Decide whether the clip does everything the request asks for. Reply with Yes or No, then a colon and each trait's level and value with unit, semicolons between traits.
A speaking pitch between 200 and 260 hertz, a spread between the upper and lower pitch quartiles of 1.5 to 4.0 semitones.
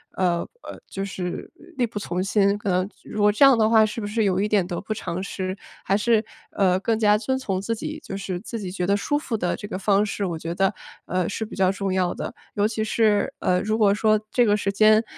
Yes: high, 205 Hz; narrow, 2.5 semitones